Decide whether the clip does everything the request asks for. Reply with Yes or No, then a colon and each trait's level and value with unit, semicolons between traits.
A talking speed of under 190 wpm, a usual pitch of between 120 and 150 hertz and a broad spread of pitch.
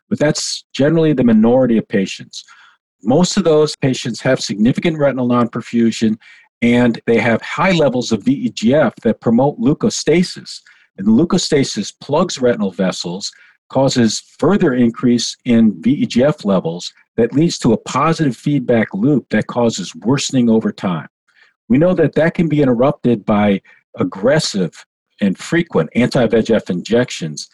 Yes: average, 140 wpm; low, 135 Hz; wide, 7.3 semitones